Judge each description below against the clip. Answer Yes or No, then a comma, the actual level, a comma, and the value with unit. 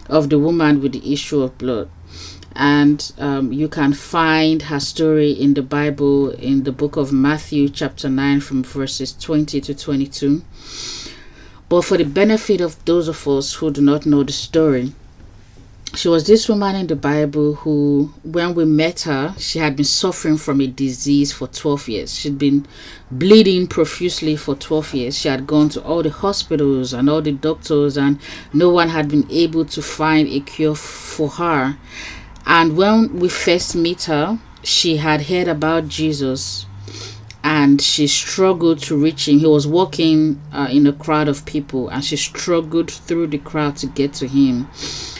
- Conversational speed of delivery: Yes, average, 175 wpm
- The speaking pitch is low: No, medium, 150 Hz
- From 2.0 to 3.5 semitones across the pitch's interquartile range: Yes, narrow, 2.4 semitones